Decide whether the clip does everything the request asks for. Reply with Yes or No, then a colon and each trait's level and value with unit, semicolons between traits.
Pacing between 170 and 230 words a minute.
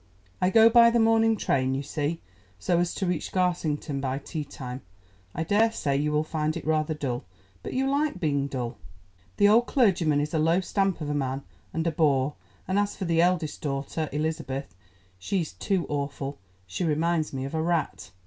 Yes: average, 185 wpm